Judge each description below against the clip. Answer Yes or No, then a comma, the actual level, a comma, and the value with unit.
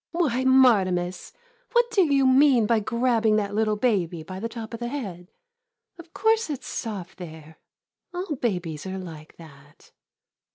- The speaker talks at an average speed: Yes, average, 170 wpm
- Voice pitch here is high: Yes, high, 220 Hz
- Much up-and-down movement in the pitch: Yes, wide, 6.6 semitones